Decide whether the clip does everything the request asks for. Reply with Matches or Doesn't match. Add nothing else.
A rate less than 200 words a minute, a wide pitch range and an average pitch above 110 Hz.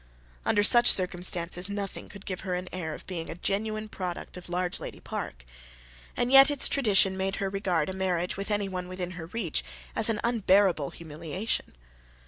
Doesn't match